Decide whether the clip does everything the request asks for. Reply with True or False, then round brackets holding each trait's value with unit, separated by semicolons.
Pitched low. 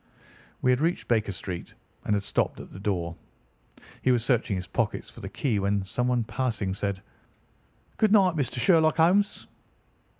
True (120 Hz)